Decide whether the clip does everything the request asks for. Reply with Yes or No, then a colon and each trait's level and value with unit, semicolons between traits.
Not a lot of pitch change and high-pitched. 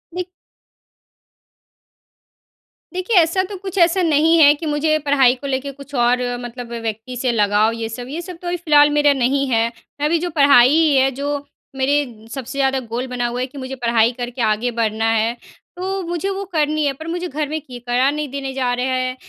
No: average, 4.1 semitones; very high, 275 Hz